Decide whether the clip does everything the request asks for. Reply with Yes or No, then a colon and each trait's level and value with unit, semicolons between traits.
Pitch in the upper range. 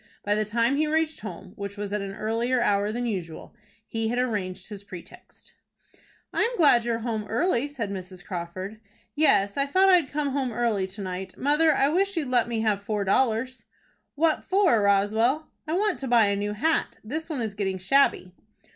Yes: high, 225 Hz